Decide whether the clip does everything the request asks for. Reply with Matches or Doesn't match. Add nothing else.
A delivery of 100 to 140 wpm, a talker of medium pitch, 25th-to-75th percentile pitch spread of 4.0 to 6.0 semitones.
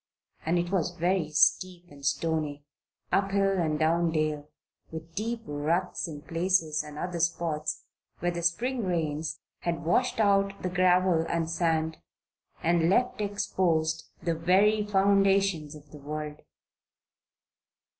Doesn't match